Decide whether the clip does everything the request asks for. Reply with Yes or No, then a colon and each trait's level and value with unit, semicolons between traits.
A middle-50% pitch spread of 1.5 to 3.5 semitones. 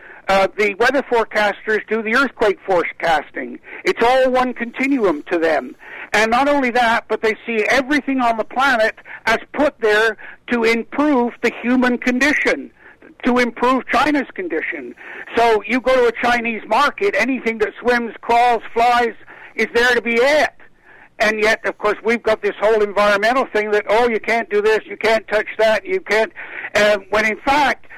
Yes: average, 3.2 semitones